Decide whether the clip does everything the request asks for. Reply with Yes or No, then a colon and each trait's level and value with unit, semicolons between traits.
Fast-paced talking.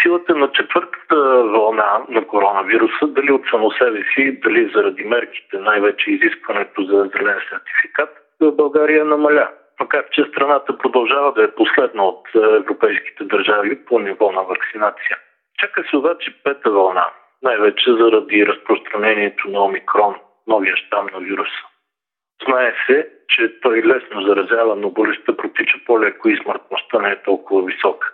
No: average, 140 wpm